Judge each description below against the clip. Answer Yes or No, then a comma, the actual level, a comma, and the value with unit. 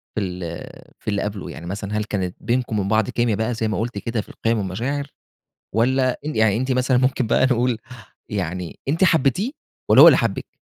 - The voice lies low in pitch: Yes, low, 110 Hz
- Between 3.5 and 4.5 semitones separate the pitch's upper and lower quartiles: Yes, average, 4.1 semitones